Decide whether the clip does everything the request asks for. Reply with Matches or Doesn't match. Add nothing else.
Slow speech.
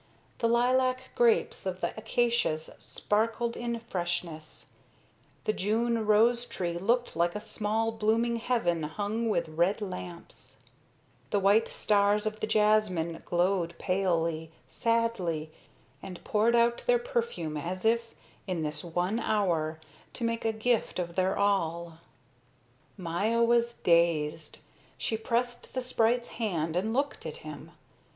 Matches